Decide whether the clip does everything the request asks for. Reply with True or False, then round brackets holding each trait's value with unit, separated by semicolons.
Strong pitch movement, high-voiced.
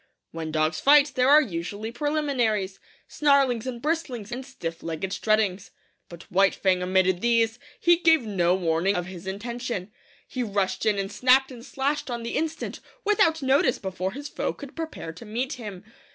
True (6.2 semitones; 230 Hz)